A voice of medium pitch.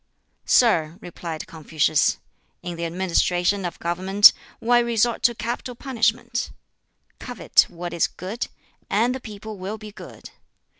No: high, 200 Hz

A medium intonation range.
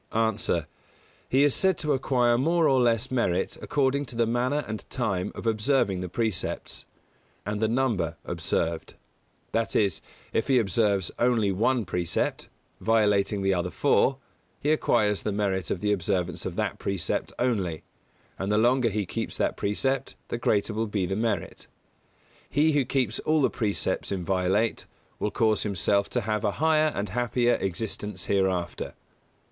Yes: average, 4.3 semitones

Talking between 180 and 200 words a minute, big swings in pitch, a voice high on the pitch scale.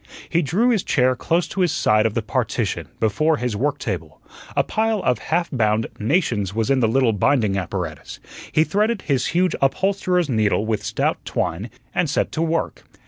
No: average, 185 wpm; wide, 7.9 semitones; low, 135 Hz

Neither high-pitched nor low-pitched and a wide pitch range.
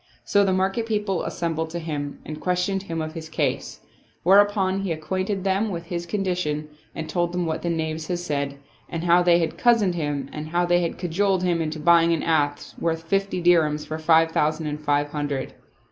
No: medium, 170 Hz; average, 2.9 semitones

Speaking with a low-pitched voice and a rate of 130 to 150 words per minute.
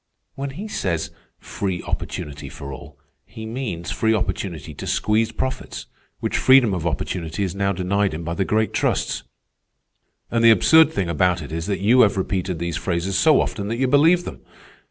No: low, 100 Hz; average, 180 wpm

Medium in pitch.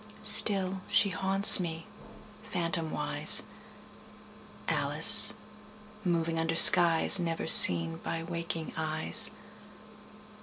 Yes: medium, 165 Hz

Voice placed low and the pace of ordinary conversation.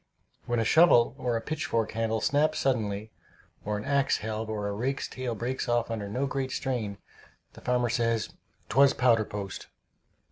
Yes: low, 115 Hz; average, 170 wpm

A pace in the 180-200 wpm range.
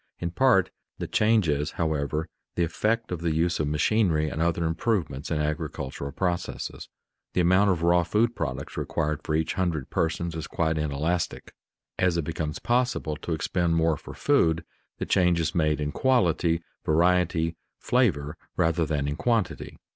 No: average, 160 wpm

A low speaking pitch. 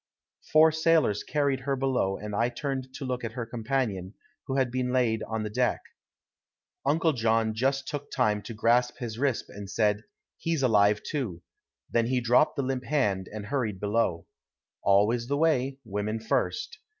Yes: low, 120 Hz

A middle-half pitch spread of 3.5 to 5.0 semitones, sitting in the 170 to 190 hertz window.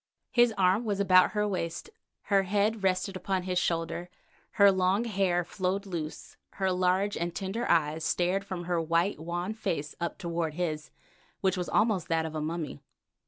No: average, 2.7 semitones; medium, 185 Hz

